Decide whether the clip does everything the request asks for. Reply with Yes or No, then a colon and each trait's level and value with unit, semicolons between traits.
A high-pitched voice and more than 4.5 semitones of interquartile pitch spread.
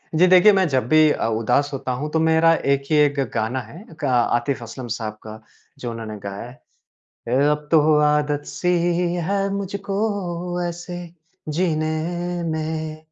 No: medium, 155 Hz; average, 5.0 semitones